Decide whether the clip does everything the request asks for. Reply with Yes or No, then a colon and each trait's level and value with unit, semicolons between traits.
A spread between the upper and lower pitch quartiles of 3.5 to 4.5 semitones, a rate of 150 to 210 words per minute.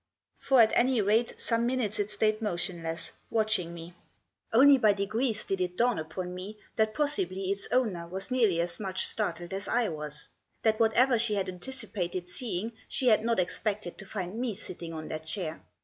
Yes: average, 4.2 semitones; average, 180 wpm